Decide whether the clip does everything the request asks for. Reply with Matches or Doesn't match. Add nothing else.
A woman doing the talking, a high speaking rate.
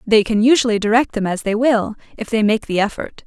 Matches